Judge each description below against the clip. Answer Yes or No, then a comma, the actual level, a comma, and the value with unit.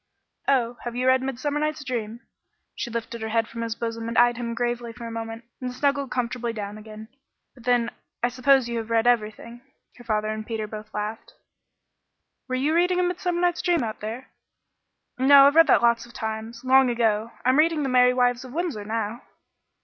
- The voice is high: Yes, high, 240 Hz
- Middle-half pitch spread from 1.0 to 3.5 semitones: Yes, narrow, 2.6 semitones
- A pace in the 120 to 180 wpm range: No, average, 195 wpm